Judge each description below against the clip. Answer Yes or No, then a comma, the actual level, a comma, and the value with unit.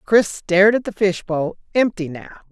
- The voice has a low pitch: No, high, 200 Hz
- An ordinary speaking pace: Yes, average, 165 wpm